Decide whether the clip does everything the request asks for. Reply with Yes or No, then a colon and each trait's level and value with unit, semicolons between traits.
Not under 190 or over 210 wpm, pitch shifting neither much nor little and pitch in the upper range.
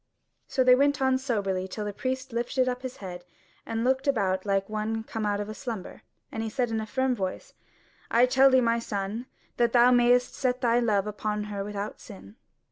Yes: average, 200 wpm; average, 3.5 semitones; high, 230 Hz